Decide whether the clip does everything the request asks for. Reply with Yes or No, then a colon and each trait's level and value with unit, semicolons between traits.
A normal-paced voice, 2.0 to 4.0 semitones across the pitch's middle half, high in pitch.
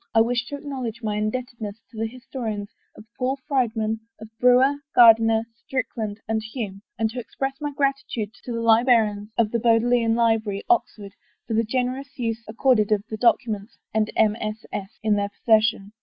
Yes: average, 175 wpm; narrow, 2.5 semitones; high, 225 Hz